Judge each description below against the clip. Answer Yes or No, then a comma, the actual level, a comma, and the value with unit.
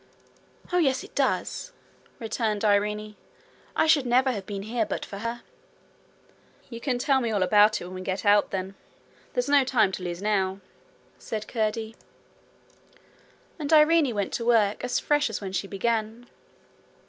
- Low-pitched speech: No, high, 220 Hz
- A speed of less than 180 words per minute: Yes, average, 160 wpm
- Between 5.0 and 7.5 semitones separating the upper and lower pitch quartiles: No, average, 3.7 semitones